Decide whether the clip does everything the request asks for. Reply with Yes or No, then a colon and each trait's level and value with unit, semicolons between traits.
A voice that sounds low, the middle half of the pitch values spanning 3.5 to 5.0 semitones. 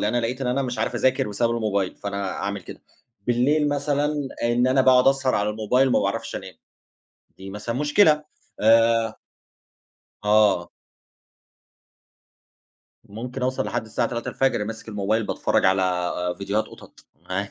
Yes: low, 115 Hz; average, 4.0 semitones